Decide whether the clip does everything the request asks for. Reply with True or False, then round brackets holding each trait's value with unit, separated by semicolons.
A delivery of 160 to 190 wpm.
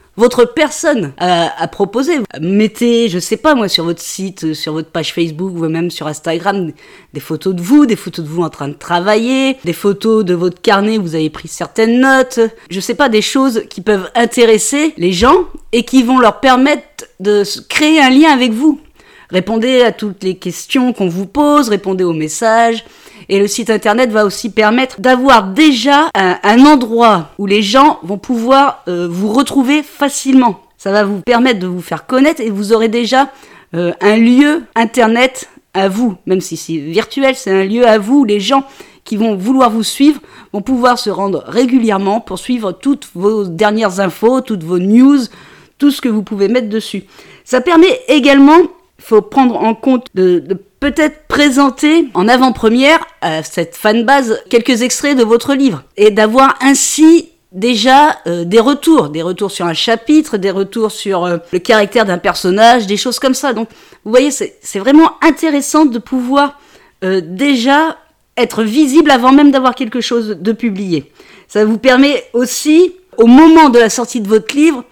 True (185 wpm)